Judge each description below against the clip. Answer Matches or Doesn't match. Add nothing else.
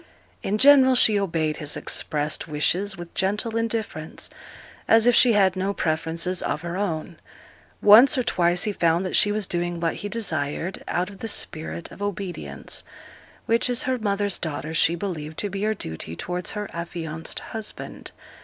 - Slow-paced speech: Doesn't match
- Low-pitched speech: Doesn't match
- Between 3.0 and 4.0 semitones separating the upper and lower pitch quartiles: Doesn't match